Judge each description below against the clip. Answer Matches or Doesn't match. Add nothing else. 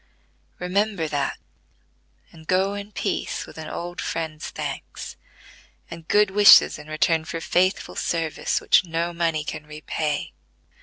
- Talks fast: Doesn't match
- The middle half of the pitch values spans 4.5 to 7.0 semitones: Doesn't match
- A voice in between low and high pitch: Matches